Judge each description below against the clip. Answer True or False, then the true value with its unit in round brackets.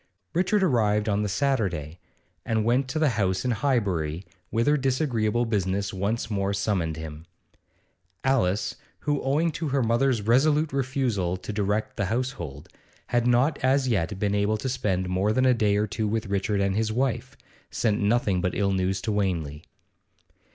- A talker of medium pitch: False (110 Hz)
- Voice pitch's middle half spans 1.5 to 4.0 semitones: False (4.8 semitones)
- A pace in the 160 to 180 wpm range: True (170 wpm)